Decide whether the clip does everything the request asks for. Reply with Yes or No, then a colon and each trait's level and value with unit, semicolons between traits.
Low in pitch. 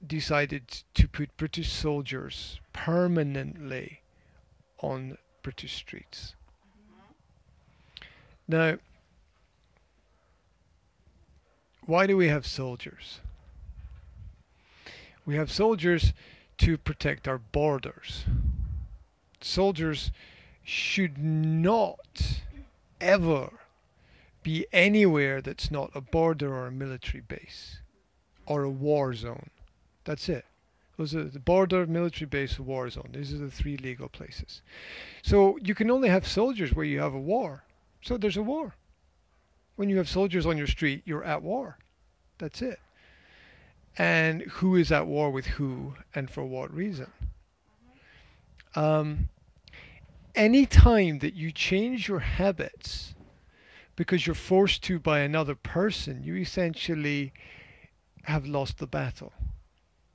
No: medium, 145 Hz